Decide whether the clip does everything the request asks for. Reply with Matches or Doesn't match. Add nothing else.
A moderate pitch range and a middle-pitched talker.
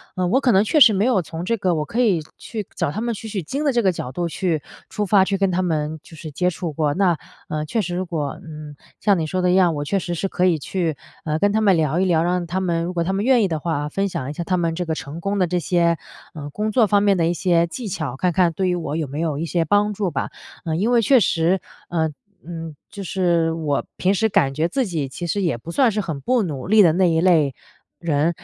Matches